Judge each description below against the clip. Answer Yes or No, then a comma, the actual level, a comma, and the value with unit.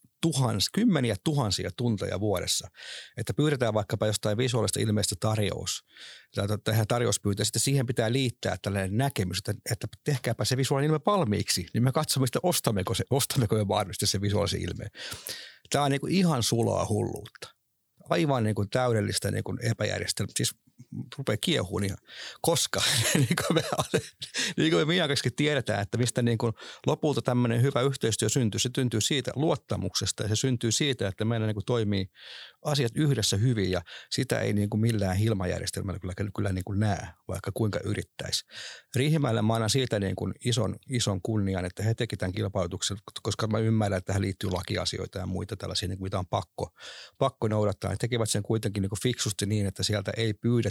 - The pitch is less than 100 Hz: No, low, 110 Hz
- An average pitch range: Yes, average, 3.8 semitones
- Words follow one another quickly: Yes, fast, 165 wpm